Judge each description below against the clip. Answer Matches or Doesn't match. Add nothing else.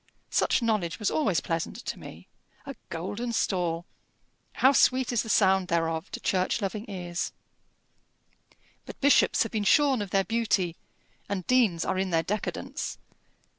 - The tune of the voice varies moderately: Matches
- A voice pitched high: Matches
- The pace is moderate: Matches